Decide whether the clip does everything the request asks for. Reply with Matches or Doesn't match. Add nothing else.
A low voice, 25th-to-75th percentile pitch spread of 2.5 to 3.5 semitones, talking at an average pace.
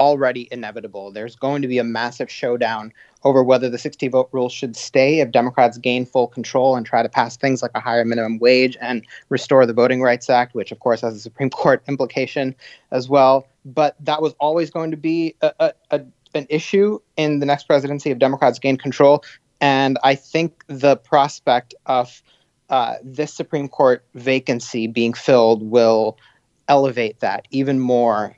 Matches